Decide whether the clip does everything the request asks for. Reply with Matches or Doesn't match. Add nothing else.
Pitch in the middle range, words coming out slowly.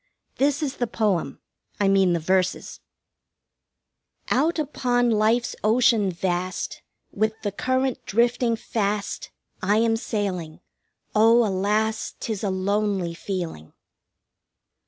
Doesn't match